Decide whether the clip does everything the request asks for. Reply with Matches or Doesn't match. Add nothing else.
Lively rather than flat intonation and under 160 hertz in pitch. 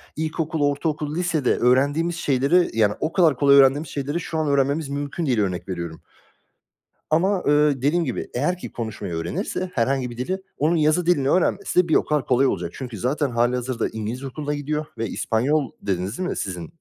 Doesn't match